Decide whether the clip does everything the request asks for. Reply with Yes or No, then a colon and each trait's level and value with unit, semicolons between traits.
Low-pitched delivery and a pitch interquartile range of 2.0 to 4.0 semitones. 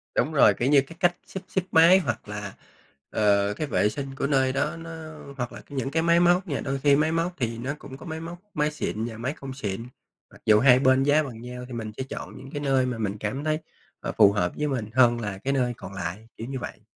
No: low, 130 Hz; average, 4.8 semitones